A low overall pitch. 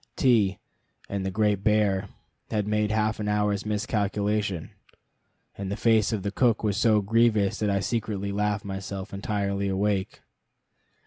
Yes: low, 105 Hz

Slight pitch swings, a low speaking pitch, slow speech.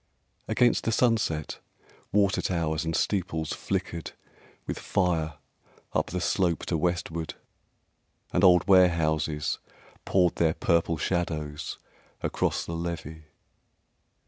Yes: narrow, 2.3 semitones; very low, 85 Hz; slow, 105 wpm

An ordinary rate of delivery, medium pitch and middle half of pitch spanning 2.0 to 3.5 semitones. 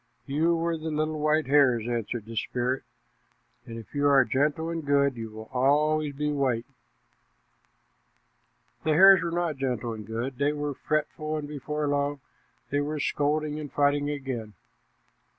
Yes: average, 155 wpm; medium, 145 Hz; average, 3.0 semitones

